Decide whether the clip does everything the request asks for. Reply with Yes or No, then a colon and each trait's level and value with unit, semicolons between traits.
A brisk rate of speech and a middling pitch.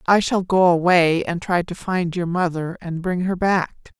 Yes: fast, 210 wpm; medium, 175 Hz